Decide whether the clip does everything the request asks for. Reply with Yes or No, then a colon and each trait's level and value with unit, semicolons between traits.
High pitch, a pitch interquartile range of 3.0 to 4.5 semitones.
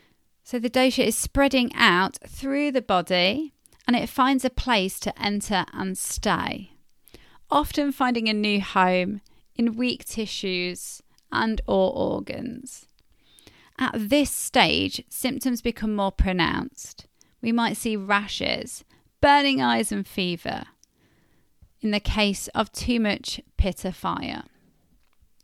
No: high, 225 Hz; average, 5.1 semitones